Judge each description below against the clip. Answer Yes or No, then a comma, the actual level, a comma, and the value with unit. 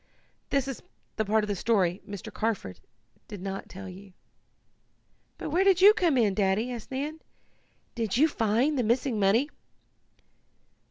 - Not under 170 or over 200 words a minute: No, average, 155 wpm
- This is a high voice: Yes, high, 225 Hz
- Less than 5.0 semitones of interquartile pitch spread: No, wide, 5.6 semitones